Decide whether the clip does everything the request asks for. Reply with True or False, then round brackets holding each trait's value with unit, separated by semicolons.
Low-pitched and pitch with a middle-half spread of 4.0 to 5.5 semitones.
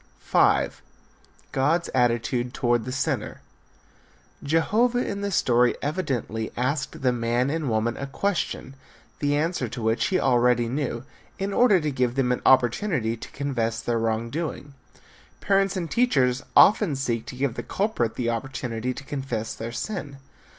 True (130 Hz; 5.2 semitones)